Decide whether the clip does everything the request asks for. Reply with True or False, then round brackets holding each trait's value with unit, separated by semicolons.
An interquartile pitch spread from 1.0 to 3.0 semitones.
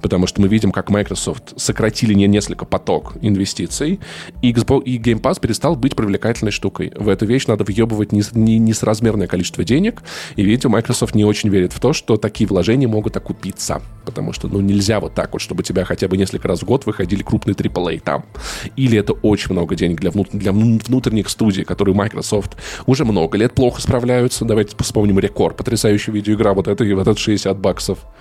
True (2.6 semitones)